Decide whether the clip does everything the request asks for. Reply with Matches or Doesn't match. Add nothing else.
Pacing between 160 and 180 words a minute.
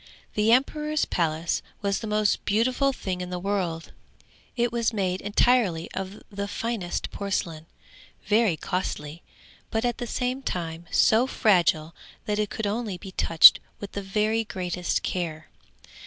Doesn't match